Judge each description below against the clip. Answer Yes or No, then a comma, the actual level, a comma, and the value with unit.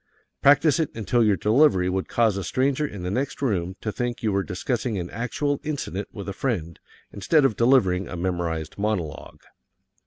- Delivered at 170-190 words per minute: Yes, average, 180 wpm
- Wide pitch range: Yes, wide, 6.0 semitones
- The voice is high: No, low, 105 Hz